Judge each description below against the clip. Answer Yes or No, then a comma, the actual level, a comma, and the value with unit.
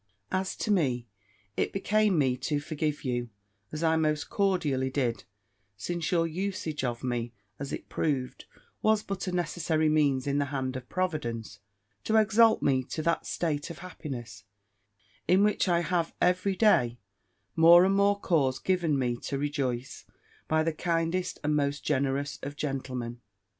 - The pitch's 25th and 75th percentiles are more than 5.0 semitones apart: Yes, wide, 5.4 semitones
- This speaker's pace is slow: No, average, 160 wpm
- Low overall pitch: No, medium, 155 Hz